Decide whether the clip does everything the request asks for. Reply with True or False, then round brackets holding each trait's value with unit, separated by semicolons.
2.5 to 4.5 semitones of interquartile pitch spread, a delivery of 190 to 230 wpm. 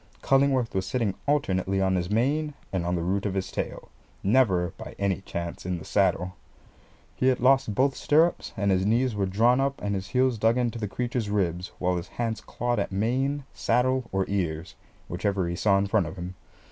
False (5.2 semitones; 200 wpm)